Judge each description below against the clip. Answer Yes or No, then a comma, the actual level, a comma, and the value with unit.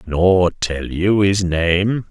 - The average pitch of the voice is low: Yes, very low, 90 Hz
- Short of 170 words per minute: Yes, average, 140 wpm